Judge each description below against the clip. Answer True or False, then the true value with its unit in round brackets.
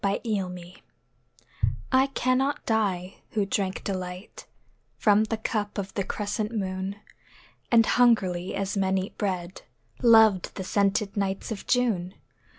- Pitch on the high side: True (200 Hz)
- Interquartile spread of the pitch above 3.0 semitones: False (2.7 semitones)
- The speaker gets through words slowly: True (130 wpm)